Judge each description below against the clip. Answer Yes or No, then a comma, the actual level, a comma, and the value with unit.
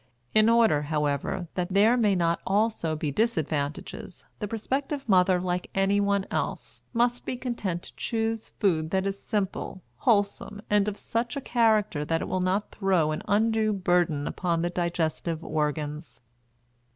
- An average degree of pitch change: Yes, average, 4.8 semitones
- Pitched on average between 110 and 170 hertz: No, high, 190 Hz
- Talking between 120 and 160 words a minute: Yes, average, 150 wpm